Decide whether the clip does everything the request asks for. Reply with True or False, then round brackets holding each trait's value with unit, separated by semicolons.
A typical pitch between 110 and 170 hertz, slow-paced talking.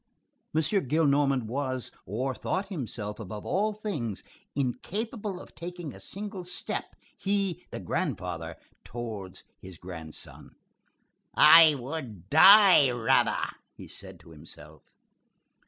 True (135 Hz; 105 wpm)